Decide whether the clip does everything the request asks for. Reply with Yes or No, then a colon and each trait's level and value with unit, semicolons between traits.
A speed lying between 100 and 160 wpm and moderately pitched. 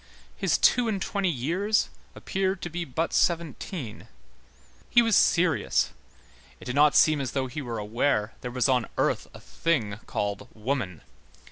Yes: average, 155 wpm; medium, 145 Hz